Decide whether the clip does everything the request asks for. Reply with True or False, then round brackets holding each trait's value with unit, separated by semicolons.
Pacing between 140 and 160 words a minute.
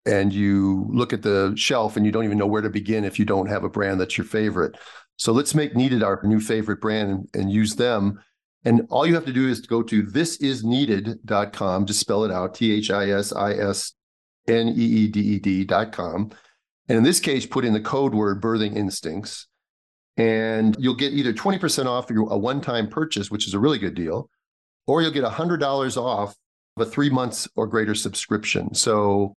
False (190 wpm)